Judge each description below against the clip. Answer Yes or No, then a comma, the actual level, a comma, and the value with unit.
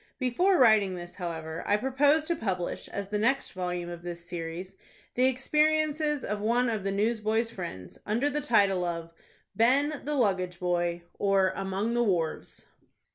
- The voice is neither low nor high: No, high, 205 Hz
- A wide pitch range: Yes, wide, 6.2 semitones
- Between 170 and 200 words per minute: No, average, 160 wpm